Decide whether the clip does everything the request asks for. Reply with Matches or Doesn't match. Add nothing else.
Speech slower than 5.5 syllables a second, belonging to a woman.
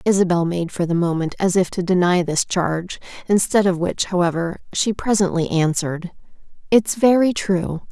Matches